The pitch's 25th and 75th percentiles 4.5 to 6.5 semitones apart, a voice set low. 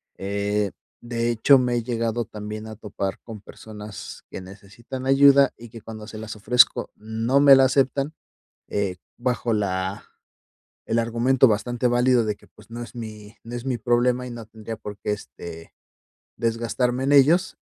No: average, 2.8 semitones; low, 115 Hz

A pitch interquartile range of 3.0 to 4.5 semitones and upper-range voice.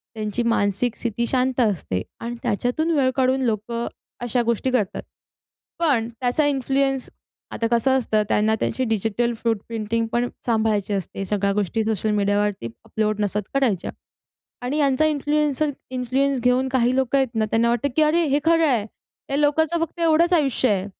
Yes: average, 4.1 semitones; high, 240 Hz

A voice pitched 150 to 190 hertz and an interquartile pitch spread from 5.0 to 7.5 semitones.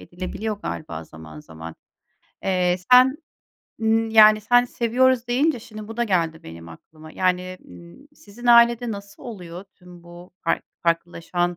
Yes: medium, 185 Hz; wide, 5.5 semitones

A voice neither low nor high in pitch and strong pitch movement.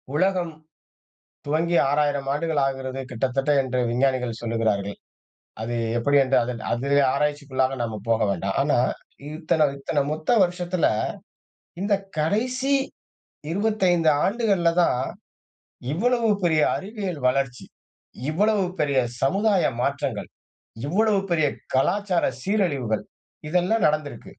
Yes: medium, 150 Hz; wide, 5.8 semitones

